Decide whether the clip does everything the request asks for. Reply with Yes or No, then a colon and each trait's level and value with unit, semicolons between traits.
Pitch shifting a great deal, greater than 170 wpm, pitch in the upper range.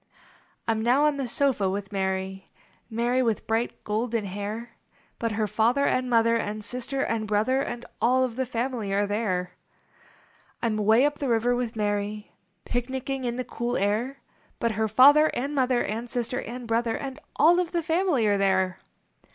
No: average, 3.4 semitones; average, 180 wpm; high, 235 Hz